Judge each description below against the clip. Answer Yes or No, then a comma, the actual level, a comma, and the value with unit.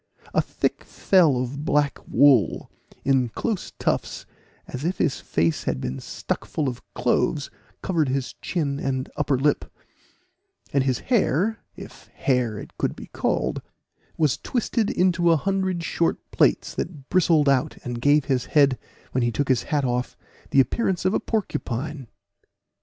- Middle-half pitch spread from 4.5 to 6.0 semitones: Yes, average, 4.9 semitones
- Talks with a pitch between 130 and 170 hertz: Yes, medium, 140 Hz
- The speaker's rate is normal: Yes, average, 155 wpm